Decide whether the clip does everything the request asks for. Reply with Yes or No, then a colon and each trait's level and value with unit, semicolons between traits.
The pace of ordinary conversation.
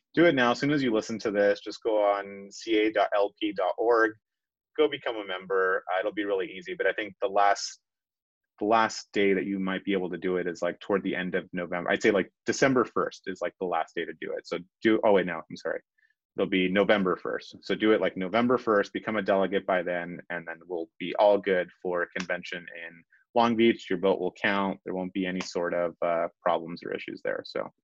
No: fast, 235 wpm